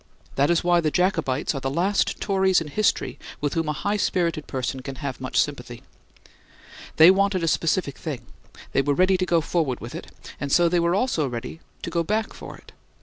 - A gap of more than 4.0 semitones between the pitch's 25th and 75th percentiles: Yes, average, 4.6 semitones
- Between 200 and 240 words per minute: Yes, fast, 205 wpm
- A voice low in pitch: No, medium, 165 Hz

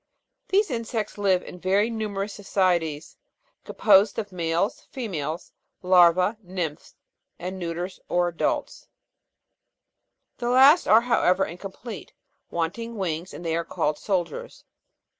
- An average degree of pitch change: Yes, average, 4.0 semitones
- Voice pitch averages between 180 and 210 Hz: Yes, high, 190 Hz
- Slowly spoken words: Yes, slow, 110 wpm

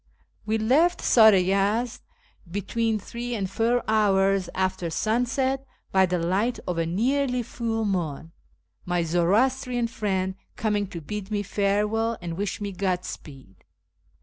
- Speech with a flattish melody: No, average, 3.9 semitones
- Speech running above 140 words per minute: No, slow, 135 wpm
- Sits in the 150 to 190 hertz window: No, high, 205 Hz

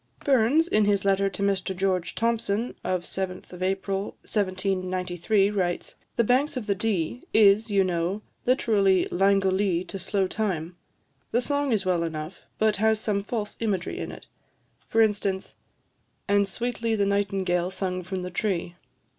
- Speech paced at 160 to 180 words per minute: No, average, 150 wpm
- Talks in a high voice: Yes, high, 195 Hz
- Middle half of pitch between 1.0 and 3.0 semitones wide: Yes, average, 2.7 semitones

